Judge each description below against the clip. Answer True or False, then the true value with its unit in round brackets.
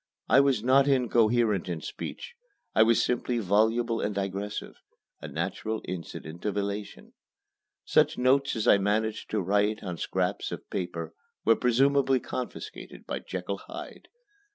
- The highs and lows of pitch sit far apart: False (3.7 semitones)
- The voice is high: False (110 Hz)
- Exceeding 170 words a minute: False (140 wpm)